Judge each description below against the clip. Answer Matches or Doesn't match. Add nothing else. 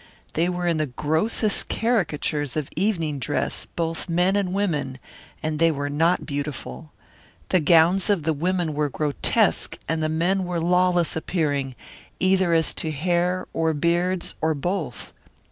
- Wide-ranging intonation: Doesn't match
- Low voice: Doesn't match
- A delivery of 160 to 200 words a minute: Doesn't match